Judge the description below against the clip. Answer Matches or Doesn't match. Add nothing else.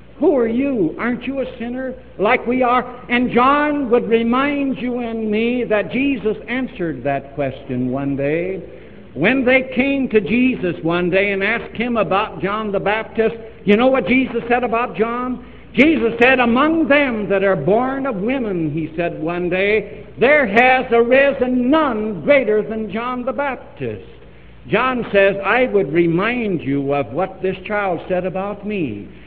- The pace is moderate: Matches